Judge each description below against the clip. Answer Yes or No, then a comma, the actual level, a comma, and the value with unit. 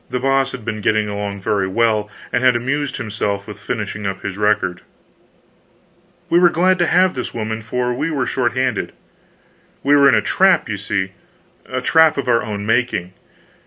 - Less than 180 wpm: No, average, 185 wpm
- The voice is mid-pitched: No, low, 115 Hz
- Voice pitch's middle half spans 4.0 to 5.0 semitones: Yes, average, 4.5 semitones